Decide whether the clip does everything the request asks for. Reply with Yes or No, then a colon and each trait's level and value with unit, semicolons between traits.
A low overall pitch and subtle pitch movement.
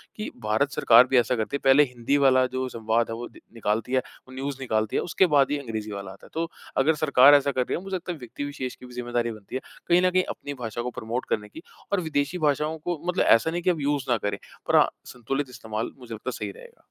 No: low, 130 Hz; average, 4.1 semitones